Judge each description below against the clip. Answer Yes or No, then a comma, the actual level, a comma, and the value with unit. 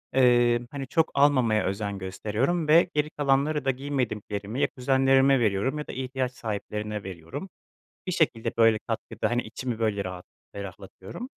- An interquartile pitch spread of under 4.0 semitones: No, average, 4.6 semitones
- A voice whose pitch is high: No, low, 125 Hz